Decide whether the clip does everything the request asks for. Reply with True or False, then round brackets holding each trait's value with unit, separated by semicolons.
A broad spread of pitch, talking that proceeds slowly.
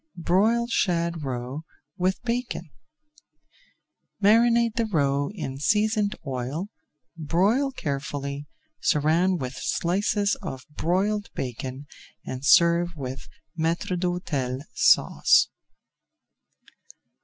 True (6.6 semitones; 85 wpm)